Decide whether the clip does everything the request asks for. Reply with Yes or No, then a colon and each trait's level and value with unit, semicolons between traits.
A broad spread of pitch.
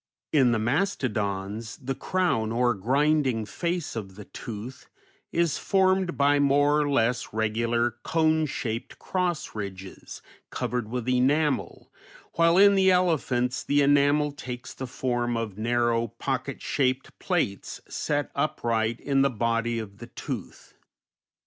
No: average, 4.2 semitones